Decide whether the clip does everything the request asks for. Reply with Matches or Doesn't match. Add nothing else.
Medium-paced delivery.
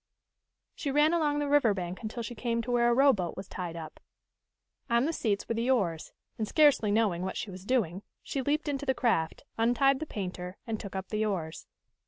Doesn't match